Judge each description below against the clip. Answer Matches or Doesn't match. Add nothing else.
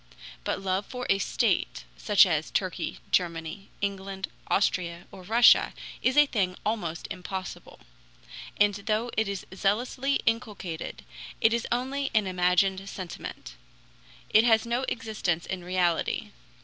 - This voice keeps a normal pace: Doesn't match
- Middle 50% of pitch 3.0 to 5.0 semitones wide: Matches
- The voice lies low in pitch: Doesn't match